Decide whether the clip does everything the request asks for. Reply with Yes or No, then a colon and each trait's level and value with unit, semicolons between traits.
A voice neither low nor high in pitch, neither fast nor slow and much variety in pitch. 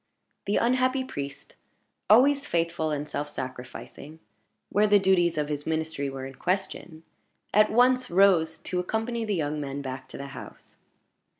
Yes: medium, 165 Hz; average, 155 wpm; wide, 6.5 semitones